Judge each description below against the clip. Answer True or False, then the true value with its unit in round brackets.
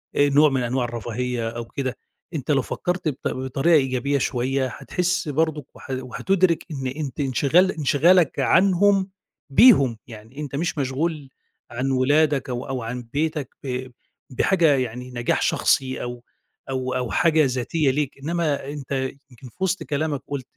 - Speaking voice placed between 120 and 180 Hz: True (140 Hz)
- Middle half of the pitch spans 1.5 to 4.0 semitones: True (3.7 semitones)